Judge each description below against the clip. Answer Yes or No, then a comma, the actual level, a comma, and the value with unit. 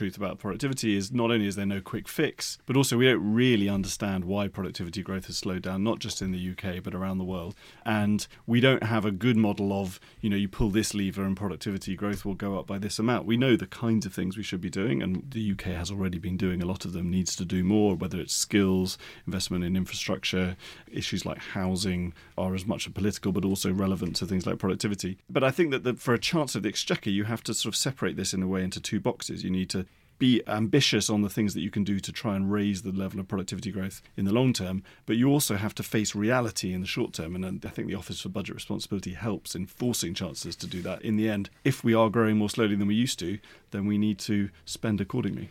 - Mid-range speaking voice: No, low, 100 Hz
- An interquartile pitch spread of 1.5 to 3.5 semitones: Yes, average, 2.8 semitones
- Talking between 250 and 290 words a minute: Yes, fast, 255 wpm